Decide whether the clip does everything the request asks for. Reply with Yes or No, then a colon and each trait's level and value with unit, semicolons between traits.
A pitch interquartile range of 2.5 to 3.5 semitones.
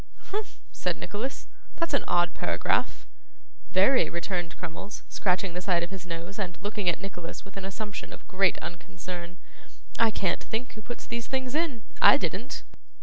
No: average, 4.0 semitones